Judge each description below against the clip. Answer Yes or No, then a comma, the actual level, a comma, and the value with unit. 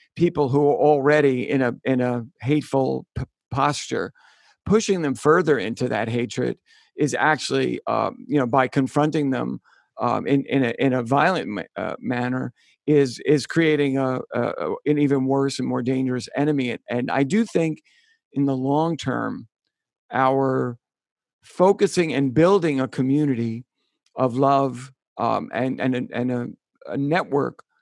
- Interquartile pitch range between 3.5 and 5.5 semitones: No, narrow, 2.6 semitones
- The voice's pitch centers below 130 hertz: No, low, 135 Hz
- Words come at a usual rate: Yes, average, 155 wpm